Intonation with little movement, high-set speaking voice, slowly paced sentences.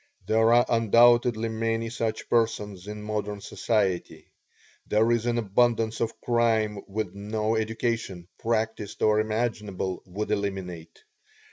No: narrow, 1.7 semitones; low, 110 Hz; slow, 120 wpm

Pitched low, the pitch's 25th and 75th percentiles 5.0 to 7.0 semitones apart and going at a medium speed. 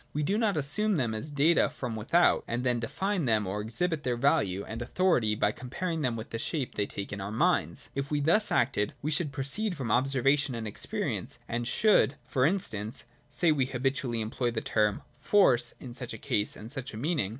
No: low, 130 Hz; wide, 5.4 semitones; fast, 215 wpm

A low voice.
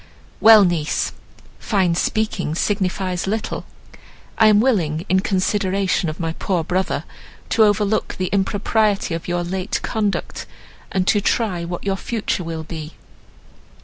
No: high, 190 Hz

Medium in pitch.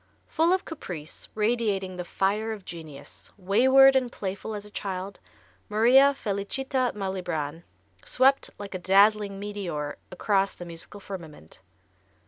No: high, 200 Hz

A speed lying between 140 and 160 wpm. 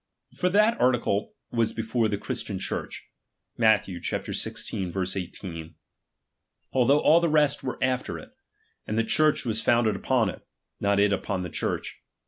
Yes: average, 145 wpm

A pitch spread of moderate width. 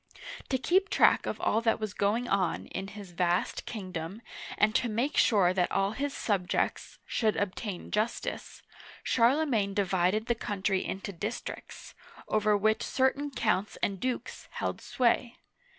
Yes: average, 3.4 semitones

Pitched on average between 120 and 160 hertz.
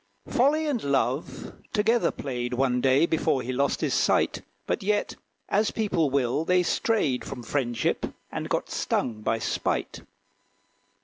Yes: medium, 140 Hz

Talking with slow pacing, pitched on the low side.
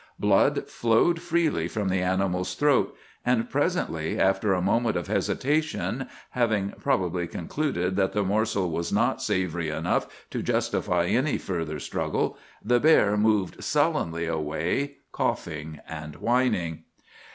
Yes: slow, 130 wpm; very low, 95 Hz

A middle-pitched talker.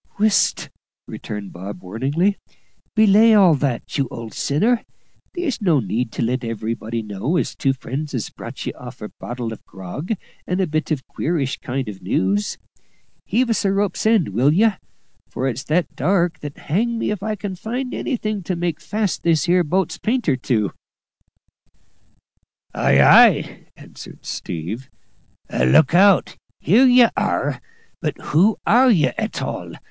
Yes: medium, 155 Hz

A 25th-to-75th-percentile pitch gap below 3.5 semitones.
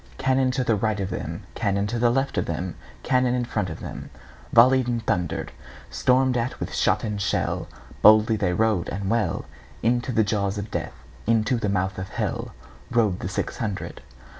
No: average, 3.8 semitones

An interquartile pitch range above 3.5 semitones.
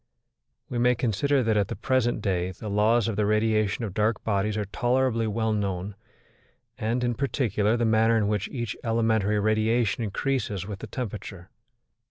No: narrow, 2.4 semitones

